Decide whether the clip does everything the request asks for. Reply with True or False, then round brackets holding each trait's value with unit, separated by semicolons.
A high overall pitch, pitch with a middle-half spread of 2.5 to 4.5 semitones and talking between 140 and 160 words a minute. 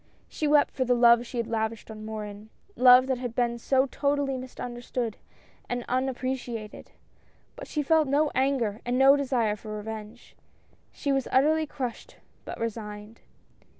True (245 Hz; 3.3 semitones; 155 wpm)